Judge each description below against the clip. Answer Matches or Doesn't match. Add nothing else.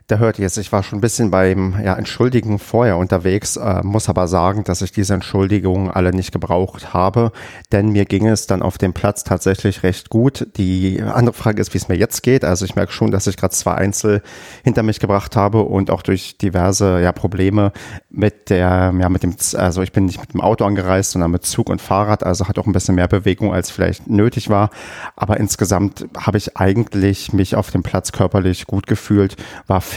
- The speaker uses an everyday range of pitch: Doesn't match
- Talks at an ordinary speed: Doesn't match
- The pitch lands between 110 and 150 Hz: Doesn't match